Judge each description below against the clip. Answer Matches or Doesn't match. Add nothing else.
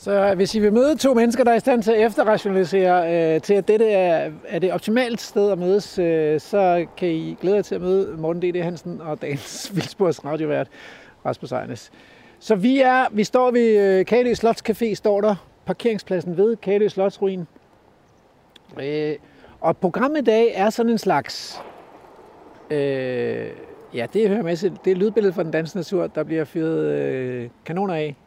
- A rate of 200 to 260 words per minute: Doesn't match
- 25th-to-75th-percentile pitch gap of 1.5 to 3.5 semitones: Doesn't match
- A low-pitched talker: Doesn't match